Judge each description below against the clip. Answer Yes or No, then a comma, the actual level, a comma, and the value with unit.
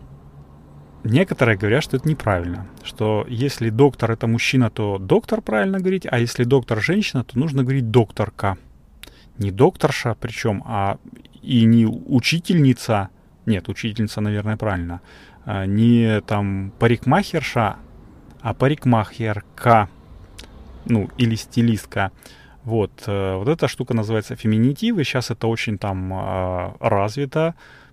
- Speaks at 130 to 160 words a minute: No, average, 115 wpm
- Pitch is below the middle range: Yes, low, 115 Hz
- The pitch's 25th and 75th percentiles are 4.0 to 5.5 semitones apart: Yes, average, 4.6 semitones